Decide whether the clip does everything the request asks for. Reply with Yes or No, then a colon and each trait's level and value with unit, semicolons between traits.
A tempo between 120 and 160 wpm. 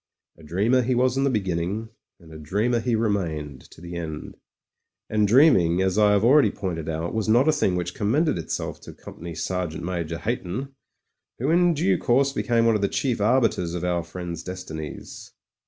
No: average, 190 wpm